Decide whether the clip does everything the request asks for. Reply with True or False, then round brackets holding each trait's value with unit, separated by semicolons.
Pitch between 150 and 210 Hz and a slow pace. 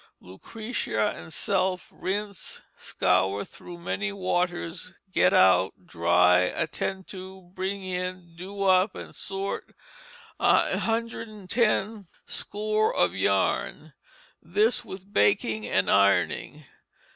True (185 Hz; 100 wpm)